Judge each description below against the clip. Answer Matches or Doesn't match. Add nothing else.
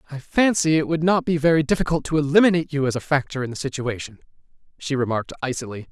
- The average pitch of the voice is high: Doesn't match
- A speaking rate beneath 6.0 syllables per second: Doesn't match